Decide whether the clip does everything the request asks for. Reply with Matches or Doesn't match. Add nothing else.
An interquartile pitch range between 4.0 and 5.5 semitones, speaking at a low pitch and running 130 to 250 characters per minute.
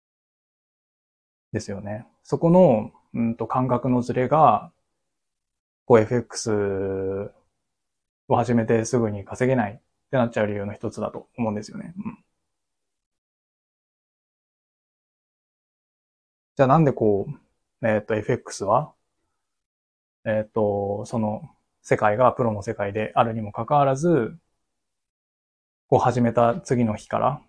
Doesn't match